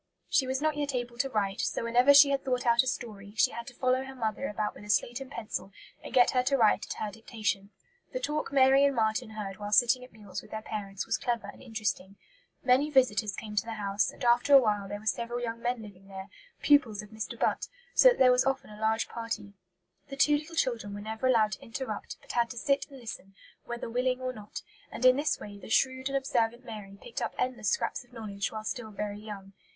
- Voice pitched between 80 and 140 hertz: No, high, 235 Hz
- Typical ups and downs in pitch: Yes, average, 3.6 semitones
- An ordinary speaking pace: No, fast, 240 wpm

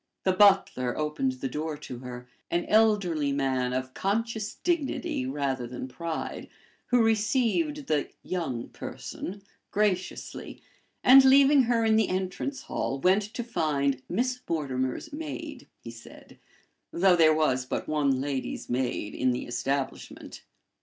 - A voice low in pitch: No, medium, 165 Hz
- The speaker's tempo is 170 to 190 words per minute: No, slow, 135 wpm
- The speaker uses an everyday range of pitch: No, wide, 9.0 semitones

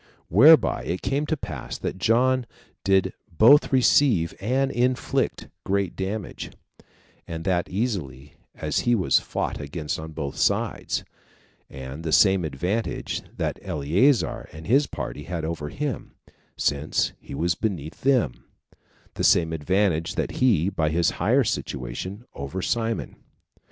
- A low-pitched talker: Yes, very low, 90 Hz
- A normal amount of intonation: No, wide, 7.1 semitones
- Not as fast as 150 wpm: Yes, slow, 135 wpm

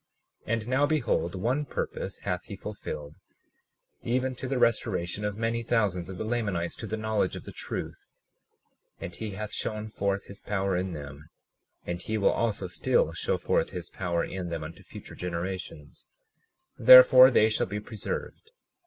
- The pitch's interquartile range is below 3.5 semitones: No, average, 4.2 semitones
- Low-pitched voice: Yes, low, 100 Hz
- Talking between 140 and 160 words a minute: No, average, 170 wpm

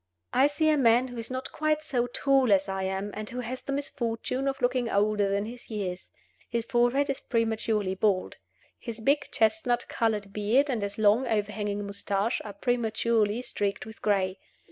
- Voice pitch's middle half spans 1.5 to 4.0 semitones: Yes, average, 3.5 semitones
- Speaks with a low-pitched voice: No, high, 225 Hz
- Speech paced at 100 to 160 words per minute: No, average, 180 wpm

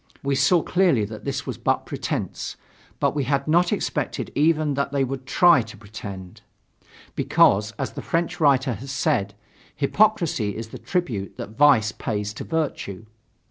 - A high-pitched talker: No, low, 135 Hz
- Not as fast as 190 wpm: Yes, average, 160 wpm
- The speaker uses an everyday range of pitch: No, wide, 6.0 semitones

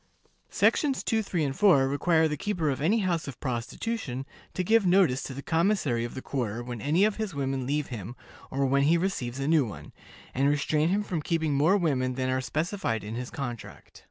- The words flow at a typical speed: No, fast, 210 wpm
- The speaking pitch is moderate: Yes, medium, 145 Hz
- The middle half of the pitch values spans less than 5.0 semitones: No, wide, 5.4 semitones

